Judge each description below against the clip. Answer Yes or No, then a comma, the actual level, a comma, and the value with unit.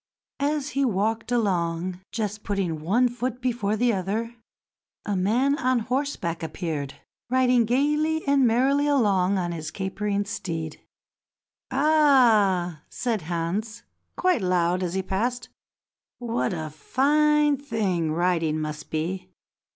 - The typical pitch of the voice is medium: No, high, 210 Hz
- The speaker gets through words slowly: Yes, slow, 120 wpm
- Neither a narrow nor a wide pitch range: No, wide, 6.3 semitones